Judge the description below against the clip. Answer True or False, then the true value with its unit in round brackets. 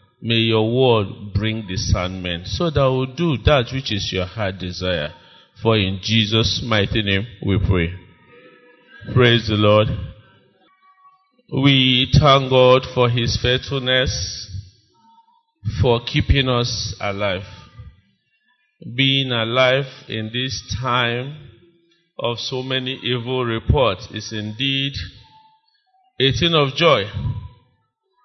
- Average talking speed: False (110 wpm)